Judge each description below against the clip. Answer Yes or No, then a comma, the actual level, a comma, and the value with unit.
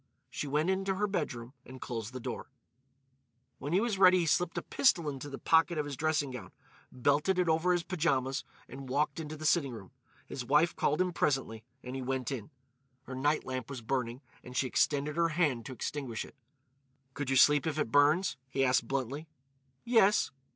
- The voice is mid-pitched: Yes, medium, 145 Hz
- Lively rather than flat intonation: No, average, 4.2 semitones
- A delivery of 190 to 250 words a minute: Yes, average, 195 wpm